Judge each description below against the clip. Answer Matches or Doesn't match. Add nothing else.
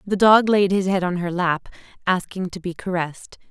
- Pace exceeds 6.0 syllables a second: Doesn't match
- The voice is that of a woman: Matches